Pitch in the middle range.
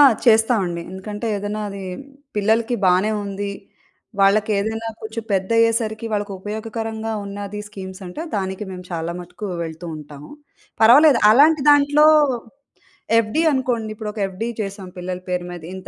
No: high, 210 Hz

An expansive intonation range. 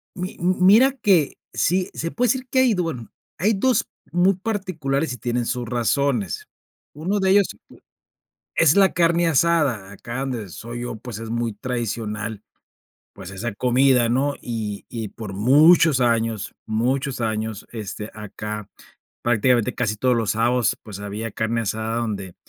Yes: wide, 7.1 semitones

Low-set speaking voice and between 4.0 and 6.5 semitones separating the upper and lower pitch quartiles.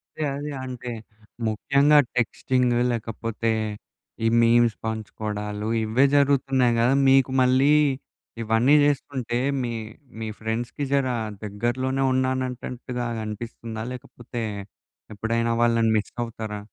No: low, 120 Hz; narrow, 2.5 semitones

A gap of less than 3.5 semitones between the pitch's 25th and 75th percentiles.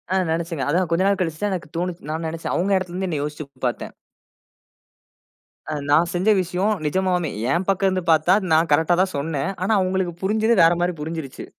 Yes: average, 2.8 semitones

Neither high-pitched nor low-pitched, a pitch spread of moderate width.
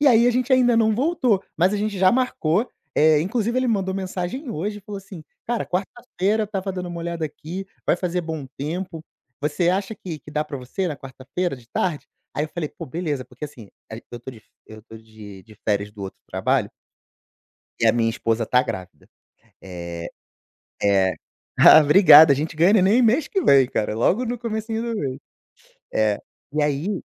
No: medium, 170 Hz; wide, 8.0 semitones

